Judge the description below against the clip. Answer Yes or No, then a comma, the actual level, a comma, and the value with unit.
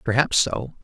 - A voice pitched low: Yes, low, 125 Hz